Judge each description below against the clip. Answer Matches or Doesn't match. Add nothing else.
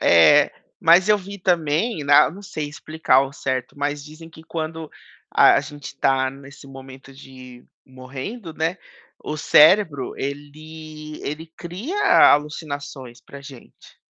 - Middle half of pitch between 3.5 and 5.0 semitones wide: Doesn't match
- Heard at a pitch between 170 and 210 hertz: Doesn't match